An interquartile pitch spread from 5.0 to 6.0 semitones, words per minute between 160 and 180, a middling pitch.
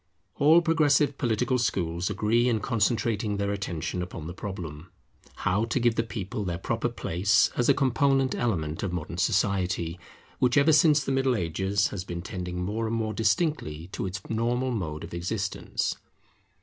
No: average, 5.3 semitones; average, 165 wpm; low, 105 Hz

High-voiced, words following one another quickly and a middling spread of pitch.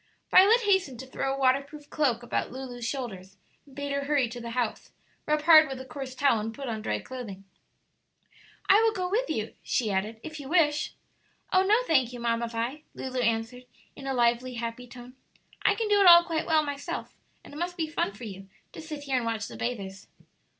Yes: very high, 260 Hz; fast, 215 wpm; average, 4.7 semitones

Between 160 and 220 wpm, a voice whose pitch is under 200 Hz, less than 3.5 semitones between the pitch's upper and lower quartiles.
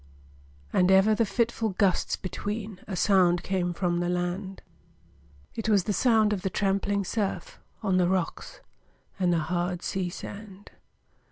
No: average, 150 wpm; high, 190 Hz; narrow, 2.6 semitones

